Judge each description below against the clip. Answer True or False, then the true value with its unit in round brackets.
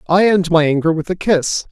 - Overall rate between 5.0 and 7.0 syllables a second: True (5.1 syllables/s)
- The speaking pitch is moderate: True (170 Hz)